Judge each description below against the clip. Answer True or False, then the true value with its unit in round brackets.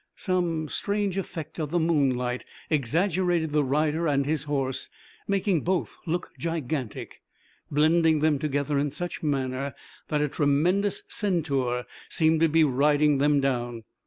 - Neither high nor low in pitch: True (150 Hz)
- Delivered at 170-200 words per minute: False (135 wpm)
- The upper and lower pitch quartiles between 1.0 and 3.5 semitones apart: True (3.2 semitones)